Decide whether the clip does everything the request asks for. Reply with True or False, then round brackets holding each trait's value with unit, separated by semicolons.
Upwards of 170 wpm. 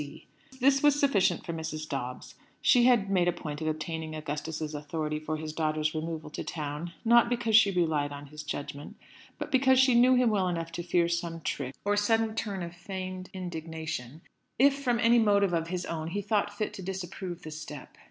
True (200 wpm)